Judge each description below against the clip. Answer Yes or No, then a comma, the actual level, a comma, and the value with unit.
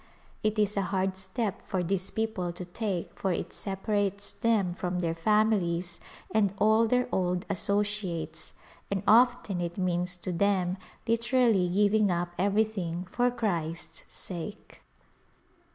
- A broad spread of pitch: No, average, 3.2 semitones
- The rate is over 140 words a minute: No, slow, 135 wpm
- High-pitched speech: Yes, high, 195 Hz